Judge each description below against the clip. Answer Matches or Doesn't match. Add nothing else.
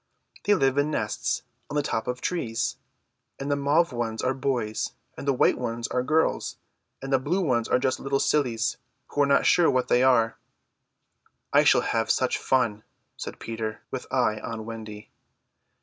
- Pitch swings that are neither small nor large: Matches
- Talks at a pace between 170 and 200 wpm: Matches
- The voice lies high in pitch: Doesn't match